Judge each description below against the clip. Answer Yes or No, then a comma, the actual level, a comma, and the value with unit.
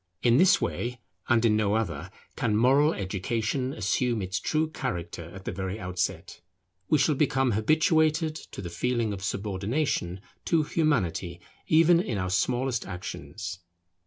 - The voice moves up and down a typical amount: No, wide, 7.2 semitones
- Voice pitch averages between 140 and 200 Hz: No, low, 115 Hz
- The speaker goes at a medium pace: Yes, average, 145 wpm